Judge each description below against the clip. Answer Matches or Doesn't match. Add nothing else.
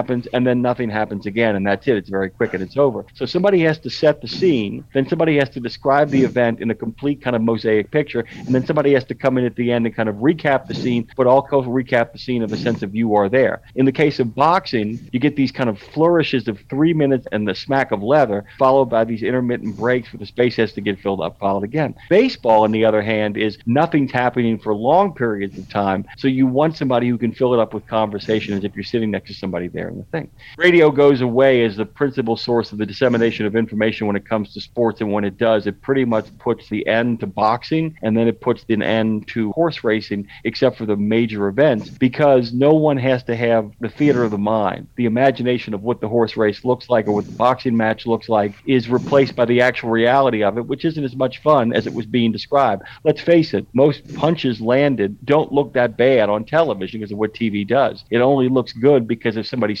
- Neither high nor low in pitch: Doesn't match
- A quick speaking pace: Matches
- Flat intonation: Doesn't match